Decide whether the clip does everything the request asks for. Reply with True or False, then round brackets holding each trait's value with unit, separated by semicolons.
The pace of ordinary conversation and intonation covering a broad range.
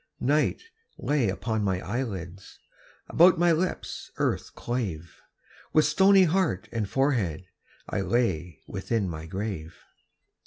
False (115 wpm; 8.2 semitones)